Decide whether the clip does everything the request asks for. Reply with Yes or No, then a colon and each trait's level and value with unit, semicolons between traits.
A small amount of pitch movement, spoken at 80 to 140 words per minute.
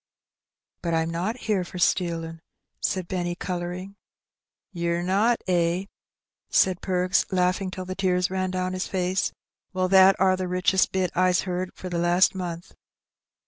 No: narrow, 1.1 semitones; average, 155 wpm